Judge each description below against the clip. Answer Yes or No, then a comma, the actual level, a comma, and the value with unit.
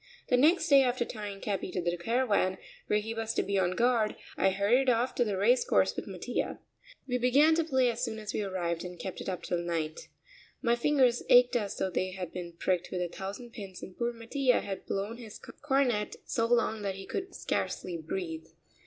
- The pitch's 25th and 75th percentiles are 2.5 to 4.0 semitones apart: No, average, 4.7 semitones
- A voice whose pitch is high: Yes, high, 215 Hz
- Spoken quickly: Yes, fast, 215 wpm